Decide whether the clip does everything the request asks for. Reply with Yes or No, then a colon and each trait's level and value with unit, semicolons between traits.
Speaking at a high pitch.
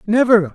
Yes: high, 215 Hz